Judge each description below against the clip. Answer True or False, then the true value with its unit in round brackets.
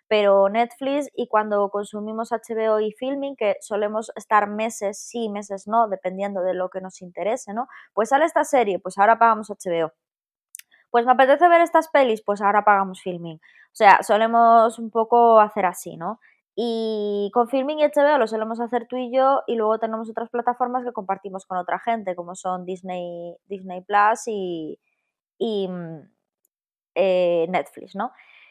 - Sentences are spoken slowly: False (165 wpm)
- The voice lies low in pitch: False (215 Hz)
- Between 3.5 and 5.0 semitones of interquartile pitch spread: True (3.8 semitones)